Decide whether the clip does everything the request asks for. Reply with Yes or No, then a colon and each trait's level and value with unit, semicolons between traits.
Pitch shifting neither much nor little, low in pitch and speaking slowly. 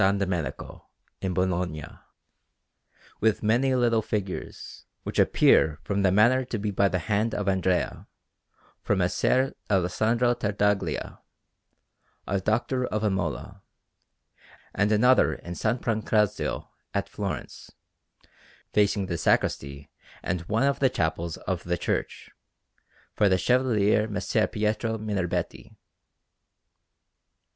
Yes: average, 3.3 semitones; low, 105 Hz; slow, 110 wpm